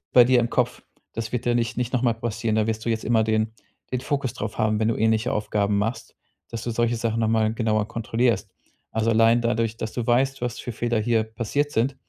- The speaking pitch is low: Yes, low, 115 Hz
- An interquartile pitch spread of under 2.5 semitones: Yes, narrow, 1.6 semitones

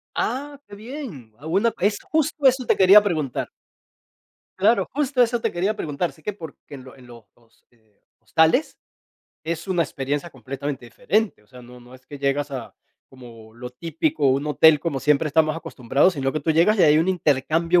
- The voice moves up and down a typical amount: No, wide, 6.5 semitones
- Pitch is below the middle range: No, medium, 155 Hz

